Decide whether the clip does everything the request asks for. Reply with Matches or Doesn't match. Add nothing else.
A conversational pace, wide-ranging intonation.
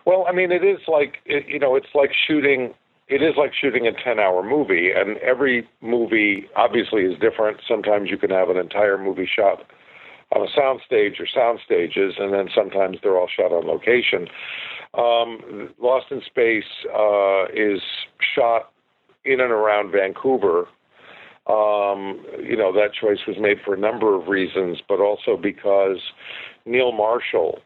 Matches